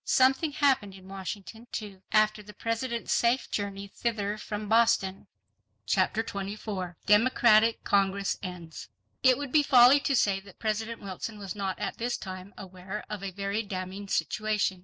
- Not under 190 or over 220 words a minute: No, average, 155 wpm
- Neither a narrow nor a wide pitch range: Yes, average, 3.1 semitones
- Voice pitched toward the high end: Yes, high, 210 Hz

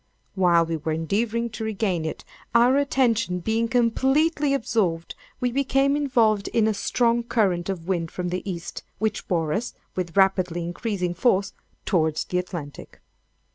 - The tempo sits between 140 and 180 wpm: Yes, average, 150 wpm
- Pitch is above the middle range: Yes, high, 200 Hz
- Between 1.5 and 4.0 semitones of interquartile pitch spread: No, average, 5.2 semitones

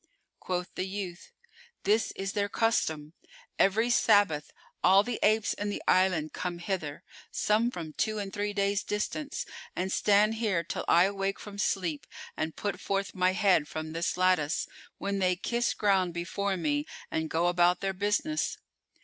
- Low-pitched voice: No, high, 195 Hz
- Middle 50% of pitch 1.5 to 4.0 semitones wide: Yes, average, 2.8 semitones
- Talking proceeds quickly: No, average, 160 wpm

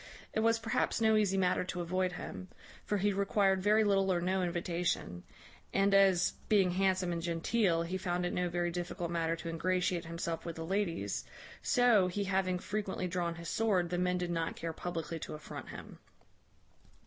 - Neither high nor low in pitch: Yes, medium, 180 Hz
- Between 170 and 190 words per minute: Yes, average, 185 wpm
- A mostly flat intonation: Yes, narrow, 2.3 semitones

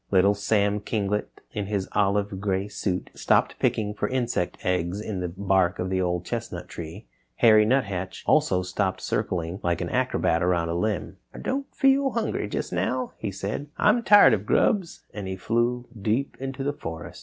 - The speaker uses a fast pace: No, average, 180 wpm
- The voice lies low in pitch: Yes, low, 100 Hz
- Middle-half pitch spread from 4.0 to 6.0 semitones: Yes, average, 4.3 semitones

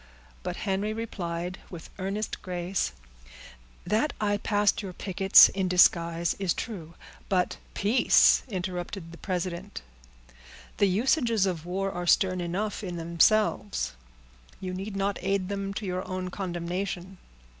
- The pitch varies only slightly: Yes, narrow, 2.3 semitones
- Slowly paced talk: Yes, slow, 130 wpm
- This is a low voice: No, high, 190 Hz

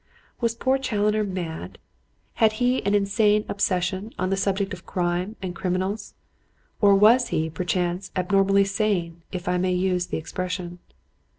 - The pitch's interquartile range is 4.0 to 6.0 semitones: No, narrow, 2.6 semitones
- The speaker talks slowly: No, average, 150 wpm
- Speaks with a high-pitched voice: Yes, high, 195 Hz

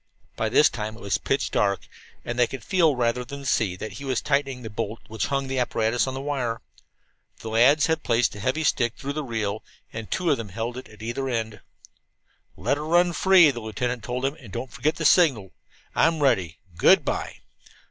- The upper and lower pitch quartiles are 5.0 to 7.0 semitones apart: No, average, 3.9 semitones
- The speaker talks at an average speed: No, fast, 210 wpm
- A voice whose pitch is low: Yes, low, 125 Hz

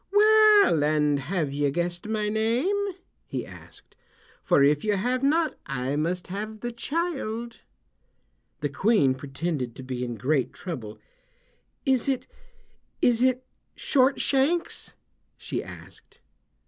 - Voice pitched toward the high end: Yes, high, 210 Hz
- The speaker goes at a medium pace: No, slow, 120 wpm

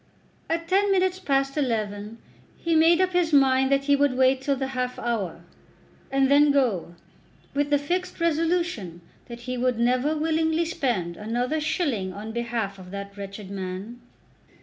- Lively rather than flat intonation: Yes, wide, 6.3 semitones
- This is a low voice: No, very high, 265 Hz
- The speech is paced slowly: No, average, 160 wpm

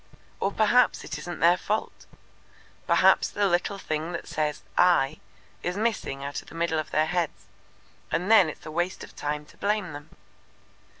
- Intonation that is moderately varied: Yes, average, 4.2 semitones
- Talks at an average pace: Yes, average, 175 wpm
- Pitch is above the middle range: No, medium, 170 Hz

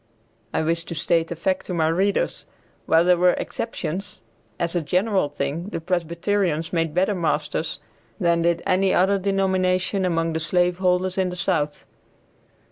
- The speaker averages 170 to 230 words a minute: No, average, 160 wpm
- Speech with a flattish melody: Yes, narrow, 2.2 semitones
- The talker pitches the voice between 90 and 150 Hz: No, medium, 175 Hz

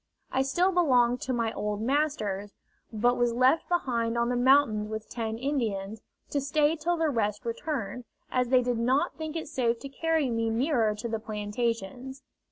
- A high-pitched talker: Yes, high, 245 Hz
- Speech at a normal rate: Yes, average, 175 wpm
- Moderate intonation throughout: Yes, average, 4.0 semitones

